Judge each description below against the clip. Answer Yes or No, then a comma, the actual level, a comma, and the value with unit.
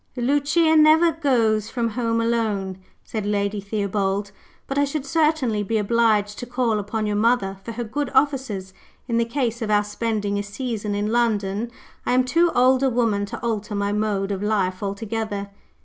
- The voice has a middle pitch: No, high, 220 Hz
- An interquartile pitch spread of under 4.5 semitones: Yes, average, 3.4 semitones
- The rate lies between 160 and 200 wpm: Yes, average, 180 wpm